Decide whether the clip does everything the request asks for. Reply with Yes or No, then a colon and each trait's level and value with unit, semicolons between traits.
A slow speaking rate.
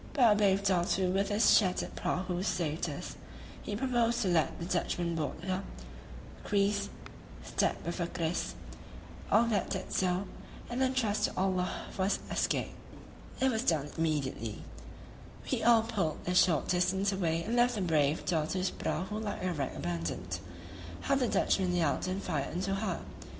No: average, 165 wpm